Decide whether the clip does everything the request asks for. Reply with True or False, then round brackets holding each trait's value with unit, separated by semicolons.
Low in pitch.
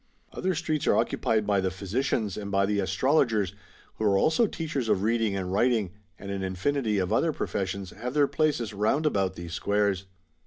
True (105 Hz)